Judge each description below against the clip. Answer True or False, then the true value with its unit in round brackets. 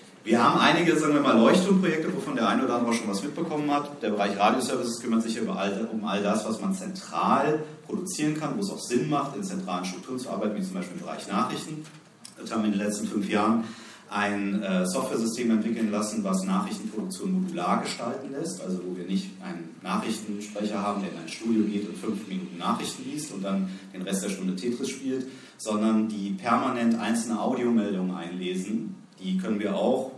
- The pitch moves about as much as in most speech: False (7.1 semitones)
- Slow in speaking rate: False (200 wpm)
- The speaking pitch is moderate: False (115 Hz)